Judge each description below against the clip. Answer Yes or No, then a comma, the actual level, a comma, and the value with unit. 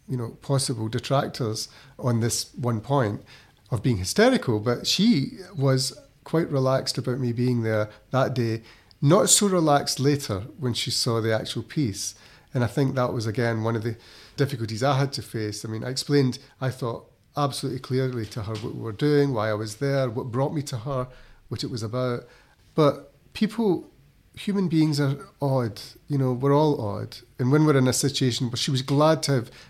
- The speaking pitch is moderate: No, low, 130 Hz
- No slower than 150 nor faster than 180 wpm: No, average, 195 wpm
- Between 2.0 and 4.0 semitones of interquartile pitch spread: Yes, average, 3.4 semitones